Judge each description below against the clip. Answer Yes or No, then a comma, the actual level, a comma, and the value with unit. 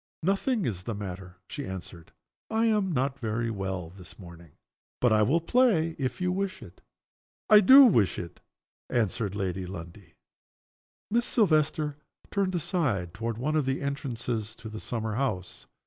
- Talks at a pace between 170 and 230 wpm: No, average, 155 wpm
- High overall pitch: No, low, 120 Hz